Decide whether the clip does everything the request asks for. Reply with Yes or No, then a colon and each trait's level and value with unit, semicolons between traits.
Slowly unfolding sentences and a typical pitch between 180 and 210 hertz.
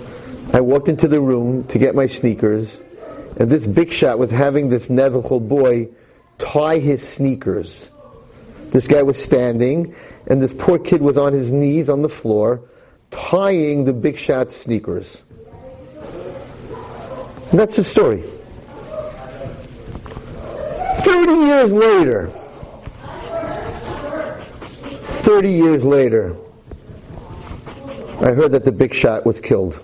No: slow, 120 wpm; medium, 140 Hz